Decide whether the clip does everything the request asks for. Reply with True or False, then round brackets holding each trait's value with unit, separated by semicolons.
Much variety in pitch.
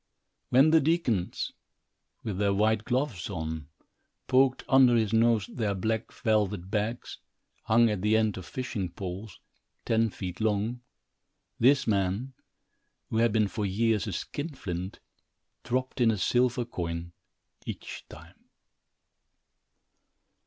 False (3.8 semitones)